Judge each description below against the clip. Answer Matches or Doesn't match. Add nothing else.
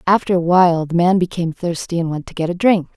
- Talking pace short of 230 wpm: Doesn't match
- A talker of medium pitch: Matches